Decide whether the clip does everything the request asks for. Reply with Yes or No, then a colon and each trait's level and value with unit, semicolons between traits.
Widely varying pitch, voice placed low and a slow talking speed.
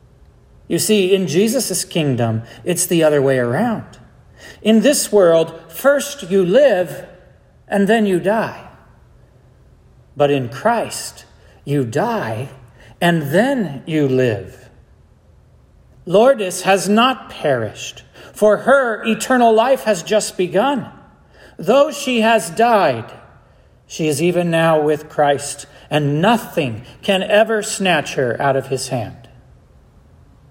No: wide, 7.7 semitones; medium, 175 Hz; slow, 120 wpm